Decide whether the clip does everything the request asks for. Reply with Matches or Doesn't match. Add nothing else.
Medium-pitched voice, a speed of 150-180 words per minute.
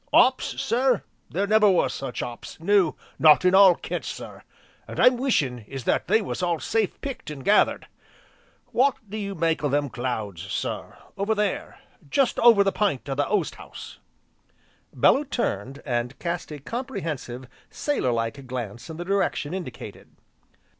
Matches